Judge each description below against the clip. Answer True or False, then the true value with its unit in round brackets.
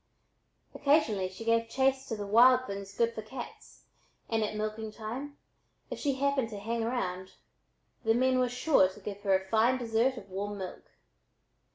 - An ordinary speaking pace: True (175 wpm)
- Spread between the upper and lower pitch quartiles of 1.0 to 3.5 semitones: False (3.9 semitones)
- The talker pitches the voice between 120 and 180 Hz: False (225 Hz)